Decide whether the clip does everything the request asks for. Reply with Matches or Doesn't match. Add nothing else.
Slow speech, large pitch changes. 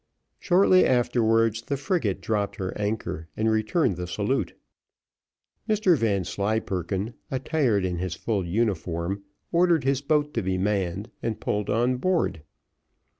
Matches